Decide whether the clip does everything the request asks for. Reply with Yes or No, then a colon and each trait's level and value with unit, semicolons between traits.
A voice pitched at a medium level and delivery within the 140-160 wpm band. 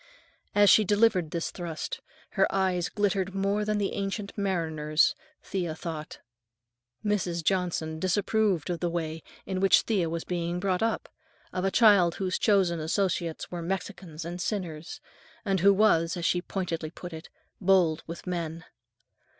Yes: medium, 180 Hz; average, 150 wpm